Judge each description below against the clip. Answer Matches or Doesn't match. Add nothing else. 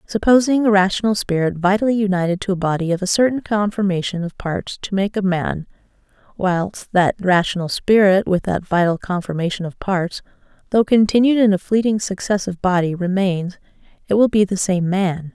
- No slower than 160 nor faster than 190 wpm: Matches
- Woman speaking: Matches